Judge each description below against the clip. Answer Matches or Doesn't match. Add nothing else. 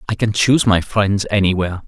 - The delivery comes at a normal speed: Matches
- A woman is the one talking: Doesn't match